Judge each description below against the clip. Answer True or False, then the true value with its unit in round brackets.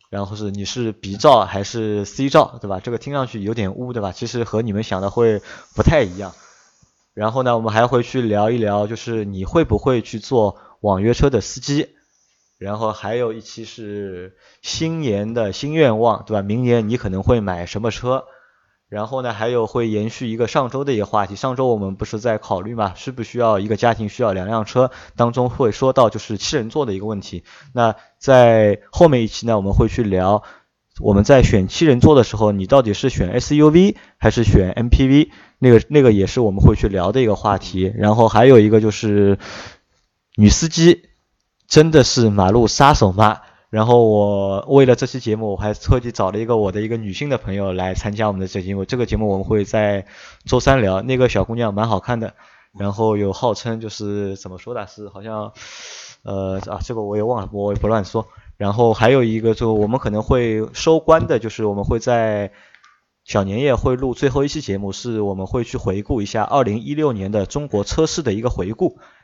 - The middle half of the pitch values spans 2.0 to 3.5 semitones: True (3.2 semitones)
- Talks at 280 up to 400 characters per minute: True (300 characters per minute)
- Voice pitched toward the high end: False (110 Hz)